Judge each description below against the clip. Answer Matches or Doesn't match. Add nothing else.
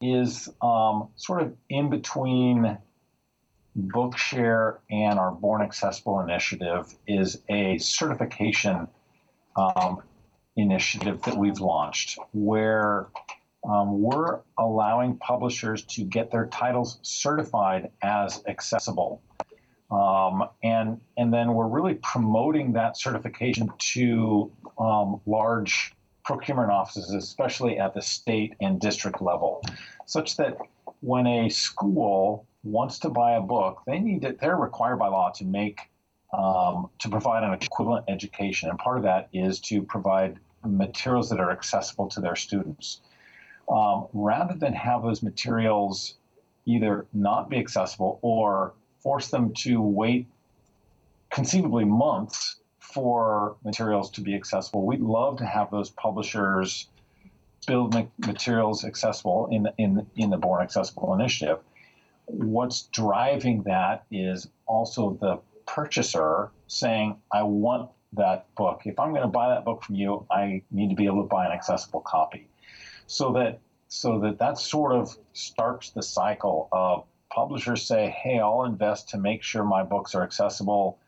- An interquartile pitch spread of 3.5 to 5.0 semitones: Doesn't match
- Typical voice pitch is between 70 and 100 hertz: Doesn't match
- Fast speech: Doesn't match